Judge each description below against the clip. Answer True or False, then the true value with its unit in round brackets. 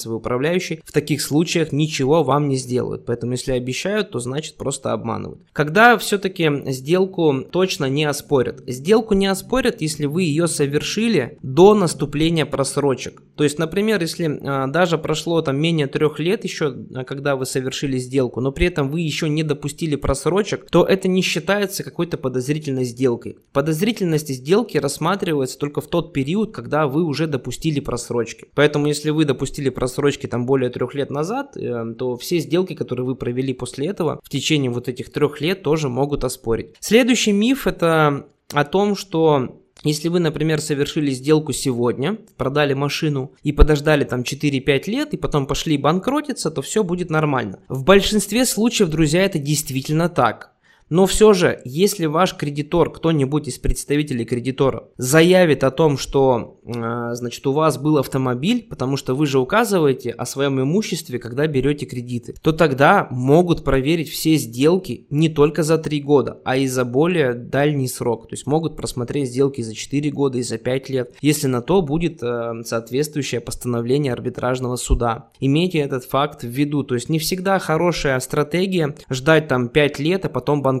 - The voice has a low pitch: False (145 Hz)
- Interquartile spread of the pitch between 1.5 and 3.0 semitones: False (3.9 semitones)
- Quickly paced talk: True (165 wpm)